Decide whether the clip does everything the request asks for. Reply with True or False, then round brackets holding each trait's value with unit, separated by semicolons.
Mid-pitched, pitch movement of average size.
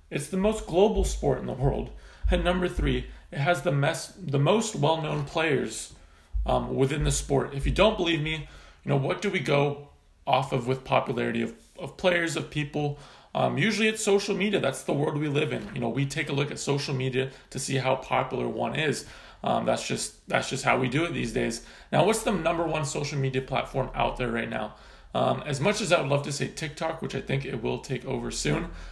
True (145 Hz; 4.6 semitones)